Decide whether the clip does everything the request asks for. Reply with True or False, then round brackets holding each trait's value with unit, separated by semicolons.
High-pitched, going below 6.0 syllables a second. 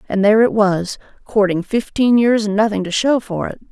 True (210 Hz; 5.3 syllables/s)